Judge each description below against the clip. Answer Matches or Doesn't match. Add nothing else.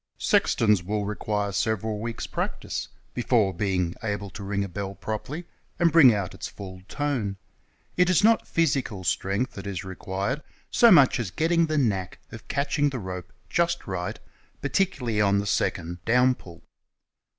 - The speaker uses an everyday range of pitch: Doesn't match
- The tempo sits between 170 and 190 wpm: Doesn't match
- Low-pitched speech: Matches